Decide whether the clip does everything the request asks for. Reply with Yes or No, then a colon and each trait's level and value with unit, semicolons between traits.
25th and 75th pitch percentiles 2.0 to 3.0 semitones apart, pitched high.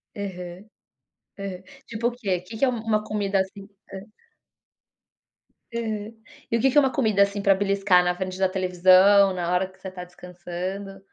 Yes: narrow, 2.4 semitones; high, 195 Hz